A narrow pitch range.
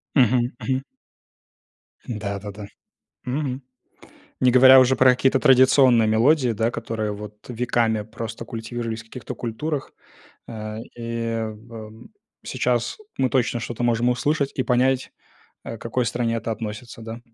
Yes: narrow, 2.3 semitones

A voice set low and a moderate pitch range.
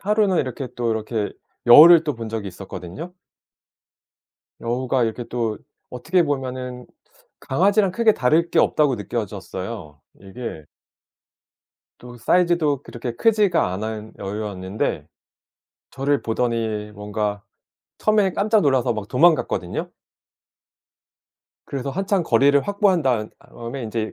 No: low, 125 Hz; wide, 7.2 semitones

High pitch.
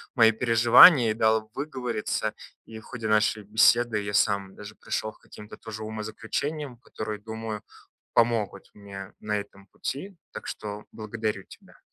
No: low, 110 Hz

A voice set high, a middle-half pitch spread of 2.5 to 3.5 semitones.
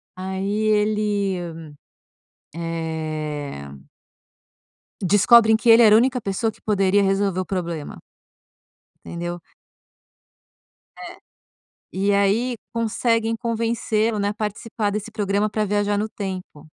Yes: high, 205 Hz; average, 2.8 semitones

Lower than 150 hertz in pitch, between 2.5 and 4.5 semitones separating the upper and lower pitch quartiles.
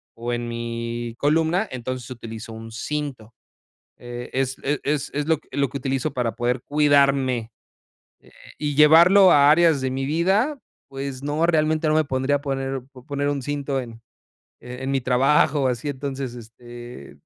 Yes: low, 135 Hz; average, 3.4 semitones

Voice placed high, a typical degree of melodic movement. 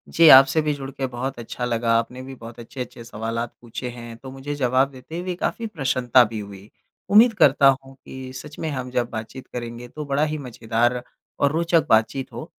No: low, 130 Hz; average, 3.2 semitones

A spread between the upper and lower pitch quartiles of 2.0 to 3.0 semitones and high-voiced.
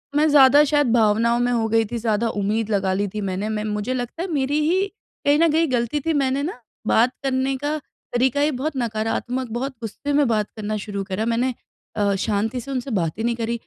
No: average, 4.2 semitones; high, 235 Hz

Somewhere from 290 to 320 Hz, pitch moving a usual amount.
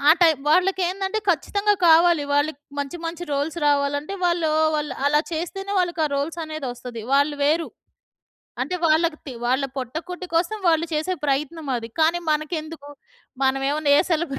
Yes: very high, 310 Hz; average, 3.2 semitones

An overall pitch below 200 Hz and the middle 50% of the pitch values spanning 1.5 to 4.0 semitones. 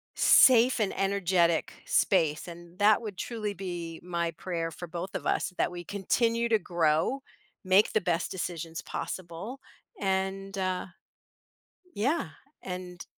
Yes: medium, 185 Hz; average, 2.9 semitones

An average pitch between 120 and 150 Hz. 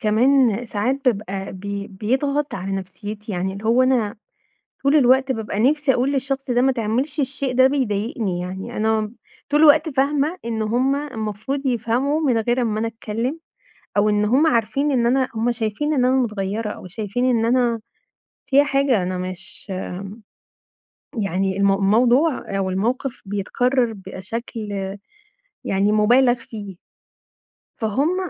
No: high, 230 Hz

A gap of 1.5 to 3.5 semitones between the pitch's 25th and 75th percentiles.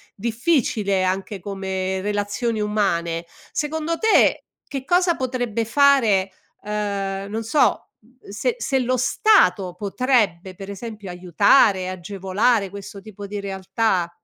No: average, 4.2 semitones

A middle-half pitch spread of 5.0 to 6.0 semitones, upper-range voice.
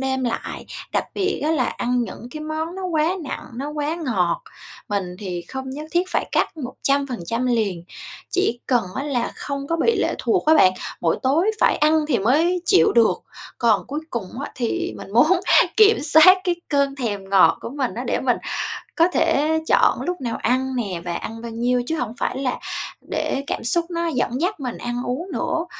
Yes: average, 5.3 semitones; very high, 265 Hz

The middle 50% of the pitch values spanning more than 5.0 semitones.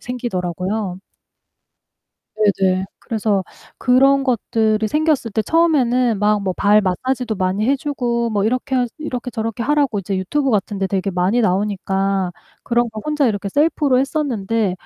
No: average, 4.7 semitones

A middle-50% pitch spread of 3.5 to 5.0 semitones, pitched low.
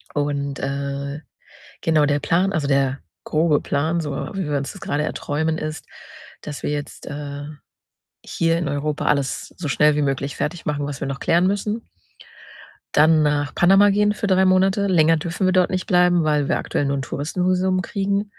No: average, 4.2 semitones; medium, 155 Hz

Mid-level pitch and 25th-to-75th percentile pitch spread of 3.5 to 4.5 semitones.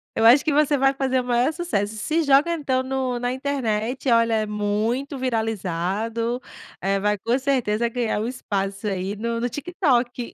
No: high, 240 Hz; average, 3.9 semitones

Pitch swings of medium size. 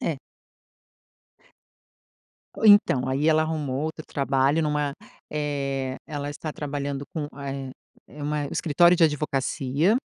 No: narrow, 2.1 semitones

